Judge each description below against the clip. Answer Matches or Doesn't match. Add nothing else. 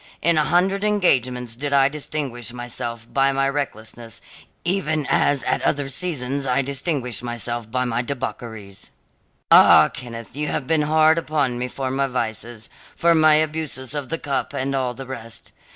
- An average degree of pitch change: Matches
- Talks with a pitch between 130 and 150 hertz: Matches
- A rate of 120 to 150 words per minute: Doesn't match